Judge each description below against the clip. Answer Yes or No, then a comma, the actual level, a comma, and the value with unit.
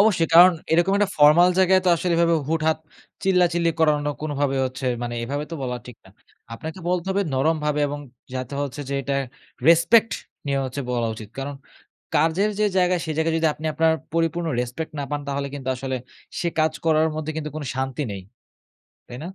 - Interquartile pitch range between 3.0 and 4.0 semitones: Yes, average, 3.5 semitones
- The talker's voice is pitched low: No, medium, 155 Hz